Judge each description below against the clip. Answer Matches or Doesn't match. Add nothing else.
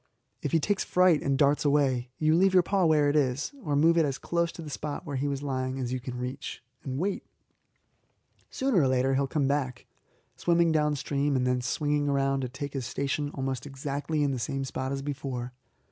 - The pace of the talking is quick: Matches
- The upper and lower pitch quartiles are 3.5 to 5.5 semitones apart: Doesn't match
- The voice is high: Doesn't match